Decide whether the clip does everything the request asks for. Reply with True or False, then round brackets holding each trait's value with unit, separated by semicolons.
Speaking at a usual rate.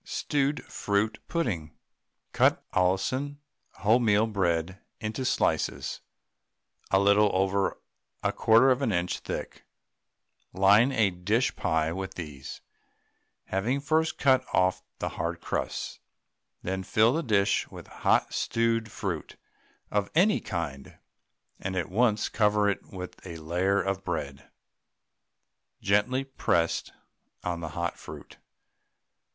False (120 wpm)